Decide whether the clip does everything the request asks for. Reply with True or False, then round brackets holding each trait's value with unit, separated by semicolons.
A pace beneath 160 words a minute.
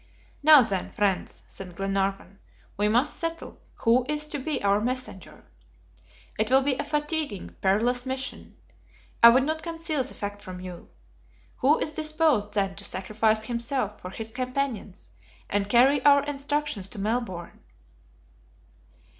True (140 wpm)